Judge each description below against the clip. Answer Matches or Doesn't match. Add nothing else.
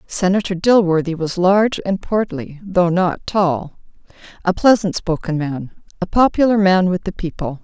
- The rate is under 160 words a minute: Matches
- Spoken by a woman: Matches